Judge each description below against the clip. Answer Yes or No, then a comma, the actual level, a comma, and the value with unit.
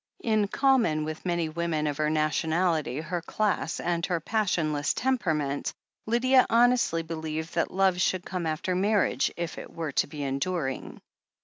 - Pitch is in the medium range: Yes, medium, 170 Hz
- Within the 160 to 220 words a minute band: No, average, 150 wpm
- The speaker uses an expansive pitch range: No, average, 4.1 semitones